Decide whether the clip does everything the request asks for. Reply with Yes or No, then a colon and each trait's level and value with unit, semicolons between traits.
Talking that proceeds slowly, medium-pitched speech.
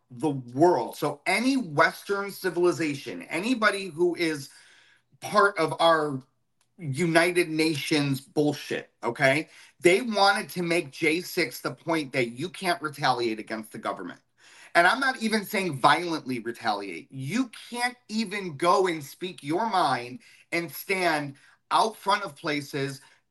Yes: slow, 130 wpm; medium, 165 Hz